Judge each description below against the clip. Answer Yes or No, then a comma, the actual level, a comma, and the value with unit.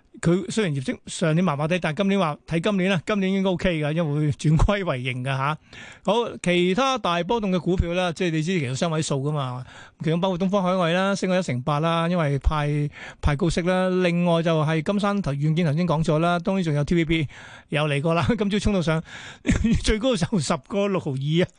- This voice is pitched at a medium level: Yes, medium, 170 Hz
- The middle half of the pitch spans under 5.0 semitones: Yes, average, 3.7 semitones